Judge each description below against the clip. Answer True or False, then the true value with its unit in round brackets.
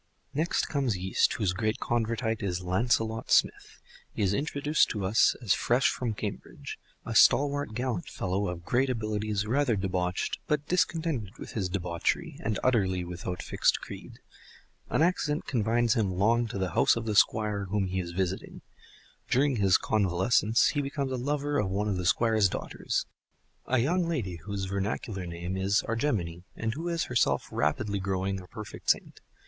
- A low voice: True (110 Hz)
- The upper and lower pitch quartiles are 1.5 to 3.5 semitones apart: False (4.9 semitones)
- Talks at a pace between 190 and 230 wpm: False (165 wpm)